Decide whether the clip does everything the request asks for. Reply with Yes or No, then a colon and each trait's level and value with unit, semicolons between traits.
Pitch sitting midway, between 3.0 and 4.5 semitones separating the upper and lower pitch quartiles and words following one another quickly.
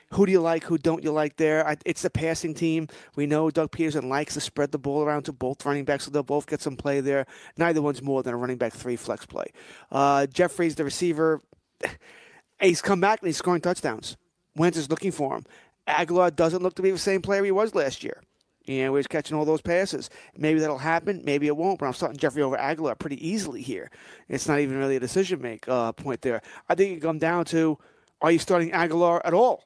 Yes: medium, 155 Hz; average, 3.4 semitones; fast, 235 wpm